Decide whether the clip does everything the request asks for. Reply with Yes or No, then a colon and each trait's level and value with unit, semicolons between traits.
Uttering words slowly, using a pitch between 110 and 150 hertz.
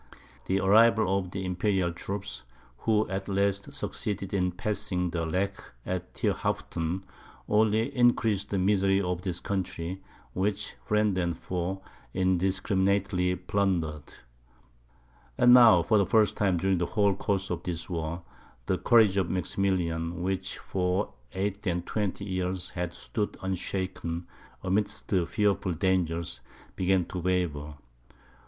No: slow, 130 wpm; very low, 95 Hz